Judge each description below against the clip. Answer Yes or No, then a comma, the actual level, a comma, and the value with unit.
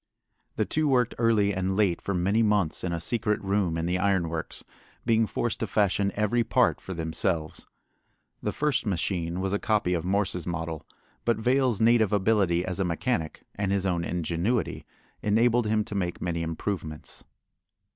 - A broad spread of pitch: No, average, 4.0 semitones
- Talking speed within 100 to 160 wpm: No, average, 170 wpm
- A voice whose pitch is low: Yes, low, 100 Hz